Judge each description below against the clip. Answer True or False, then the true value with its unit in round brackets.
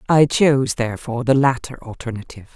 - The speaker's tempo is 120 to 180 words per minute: True (140 wpm)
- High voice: False (130 Hz)